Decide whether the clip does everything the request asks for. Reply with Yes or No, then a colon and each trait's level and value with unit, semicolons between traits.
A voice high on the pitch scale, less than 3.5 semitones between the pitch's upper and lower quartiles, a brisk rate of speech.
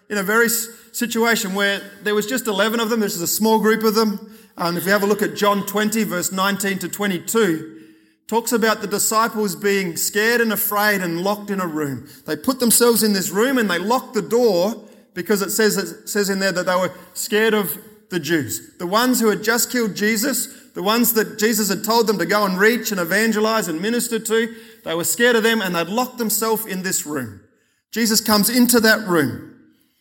Yes: high, 215 Hz; narrow, 2.6 semitones; fast, 220 wpm